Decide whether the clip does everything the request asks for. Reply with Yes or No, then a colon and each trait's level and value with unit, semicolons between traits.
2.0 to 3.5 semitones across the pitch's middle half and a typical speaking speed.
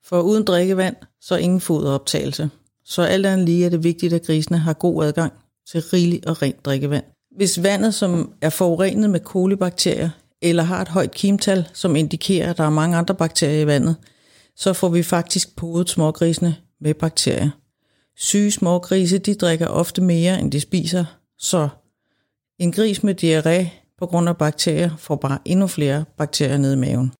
Yes: average, 3.2 semitones; average, 175 wpm